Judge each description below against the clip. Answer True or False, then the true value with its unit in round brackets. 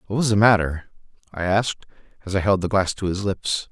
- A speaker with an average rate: False (225 wpm)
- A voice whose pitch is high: False (95 Hz)